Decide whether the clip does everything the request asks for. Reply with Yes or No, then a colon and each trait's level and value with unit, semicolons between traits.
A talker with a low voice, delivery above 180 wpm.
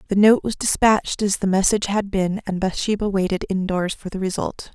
No: high, 195 Hz; average, 200 wpm